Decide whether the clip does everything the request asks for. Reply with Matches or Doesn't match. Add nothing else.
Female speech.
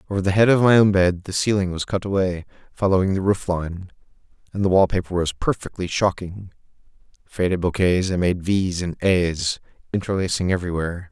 Doesn't match